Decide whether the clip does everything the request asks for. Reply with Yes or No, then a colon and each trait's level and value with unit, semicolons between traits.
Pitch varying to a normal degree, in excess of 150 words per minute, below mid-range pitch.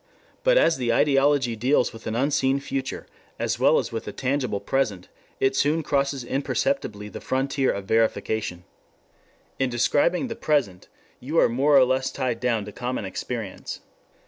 Yes: average, 3.6 semitones; average, 160 wpm; low, 130 Hz